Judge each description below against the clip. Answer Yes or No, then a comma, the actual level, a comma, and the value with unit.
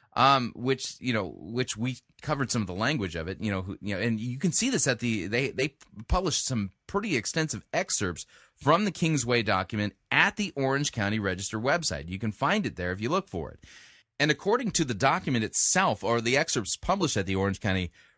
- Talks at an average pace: No, fast, 220 wpm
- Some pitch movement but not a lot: No, wide, 6.4 semitones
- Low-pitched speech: Yes, low, 120 Hz